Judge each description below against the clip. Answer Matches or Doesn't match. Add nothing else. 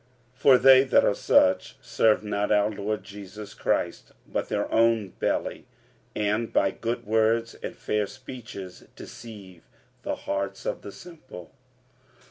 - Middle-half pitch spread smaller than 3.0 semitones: Matches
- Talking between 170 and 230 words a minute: Doesn't match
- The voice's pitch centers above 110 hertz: Doesn't match